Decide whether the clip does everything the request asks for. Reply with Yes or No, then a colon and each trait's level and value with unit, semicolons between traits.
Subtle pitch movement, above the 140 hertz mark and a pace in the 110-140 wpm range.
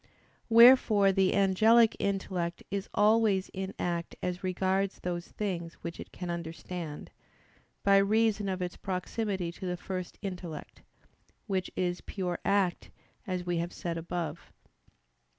Yes: narrow, 2.2 semitones; medium, 185 Hz; slow, 135 wpm